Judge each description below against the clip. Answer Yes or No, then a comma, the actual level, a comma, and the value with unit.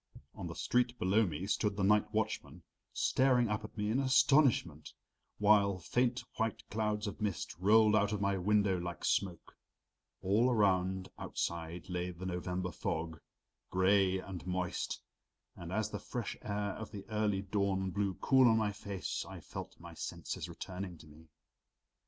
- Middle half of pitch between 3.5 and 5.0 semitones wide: No, average, 2.8 semitones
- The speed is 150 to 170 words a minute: Yes, average, 160 wpm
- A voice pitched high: No, low, 100 Hz